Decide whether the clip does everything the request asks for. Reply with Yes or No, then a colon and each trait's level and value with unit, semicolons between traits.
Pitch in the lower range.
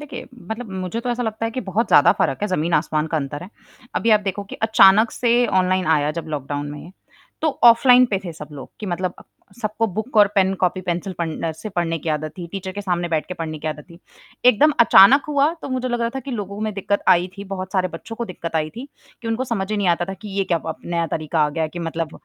No: high, 190 Hz